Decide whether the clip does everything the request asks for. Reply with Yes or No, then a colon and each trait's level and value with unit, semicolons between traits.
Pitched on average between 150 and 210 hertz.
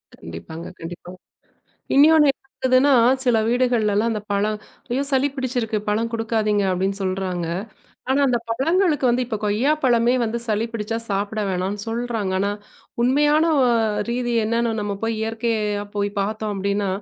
No: high, 225 Hz